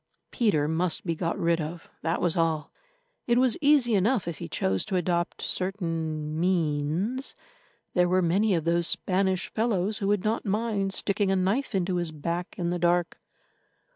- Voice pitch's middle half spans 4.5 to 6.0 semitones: No, average, 3.4 semitones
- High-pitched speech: No, medium, 180 Hz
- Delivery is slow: No, average, 170 wpm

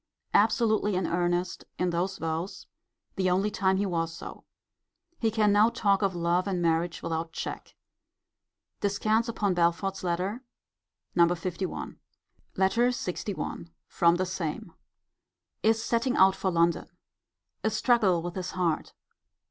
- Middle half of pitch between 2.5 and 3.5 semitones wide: Yes, average, 3.2 semitones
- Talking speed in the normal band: No, slow, 130 wpm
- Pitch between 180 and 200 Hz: Yes, medium, 185 Hz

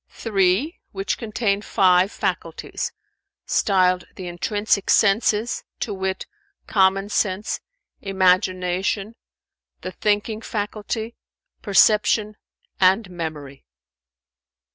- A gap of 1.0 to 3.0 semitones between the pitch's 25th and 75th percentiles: Yes, narrow, 2.4 semitones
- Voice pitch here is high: Yes, high, 195 Hz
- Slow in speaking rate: Yes, slow, 80 wpm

